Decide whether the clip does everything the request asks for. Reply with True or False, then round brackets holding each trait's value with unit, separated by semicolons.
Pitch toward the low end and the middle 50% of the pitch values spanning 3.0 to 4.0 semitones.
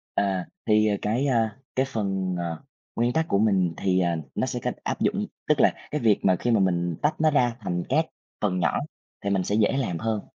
False (105 Hz; 4.5 semitones)